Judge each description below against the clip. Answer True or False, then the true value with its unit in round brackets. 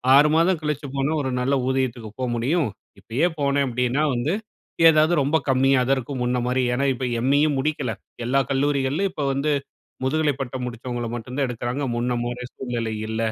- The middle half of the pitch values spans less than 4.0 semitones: True (2.8 semitones)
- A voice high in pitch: False (130 Hz)